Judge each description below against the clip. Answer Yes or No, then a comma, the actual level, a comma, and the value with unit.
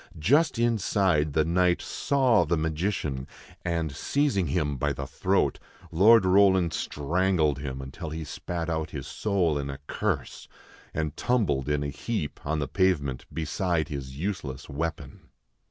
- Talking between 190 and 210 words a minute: No, average, 145 wpm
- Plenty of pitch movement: No, average, 4.7 semitones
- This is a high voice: No, very low, 80 Hz